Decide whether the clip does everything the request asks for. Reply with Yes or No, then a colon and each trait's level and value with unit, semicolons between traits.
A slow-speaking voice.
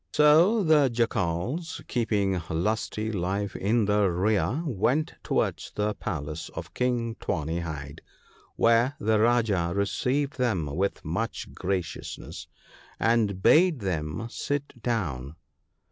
Yes: slow, 115 wpm